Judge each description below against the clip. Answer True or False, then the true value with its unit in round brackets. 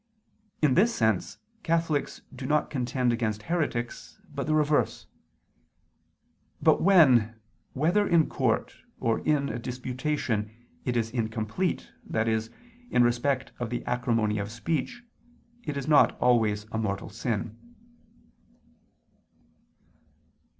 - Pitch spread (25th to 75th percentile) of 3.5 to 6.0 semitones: True (5.1 semitones)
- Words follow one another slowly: True (115 wpm)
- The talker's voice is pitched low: True (125 Hz)